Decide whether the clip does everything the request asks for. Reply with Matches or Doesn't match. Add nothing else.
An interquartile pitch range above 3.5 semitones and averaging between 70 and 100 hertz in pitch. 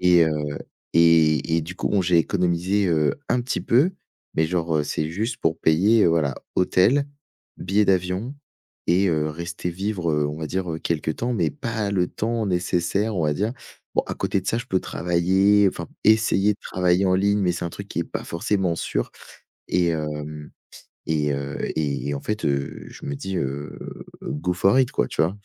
Matches